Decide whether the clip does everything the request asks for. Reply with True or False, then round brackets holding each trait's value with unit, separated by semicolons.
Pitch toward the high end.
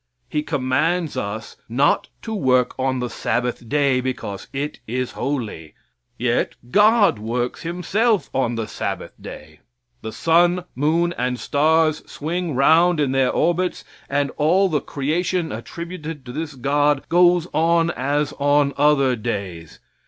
False (145 Hz)